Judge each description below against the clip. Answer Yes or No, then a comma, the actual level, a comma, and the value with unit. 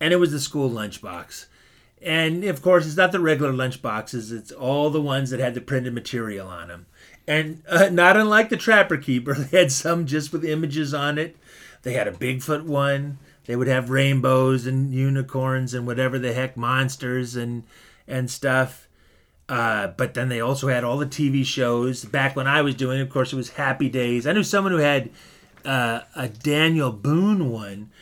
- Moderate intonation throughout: Yes, average, 3.5 semitones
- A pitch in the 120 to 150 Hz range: Yes, low, 135 Hz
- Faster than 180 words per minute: Yes, average, 195 wpm